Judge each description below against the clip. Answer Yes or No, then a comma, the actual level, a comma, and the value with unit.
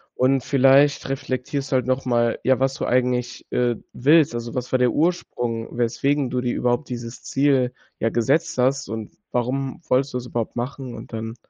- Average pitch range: No, narrow, 2.0 semitones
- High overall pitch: No, low, 125 Hz